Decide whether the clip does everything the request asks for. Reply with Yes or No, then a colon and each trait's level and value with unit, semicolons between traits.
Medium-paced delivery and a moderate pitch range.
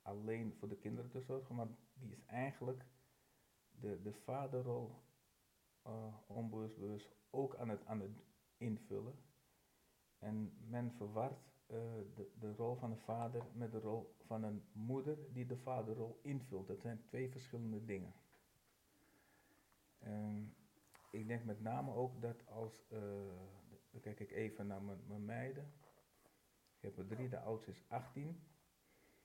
Yes: average, 145 wpm; average, 3.2 semitones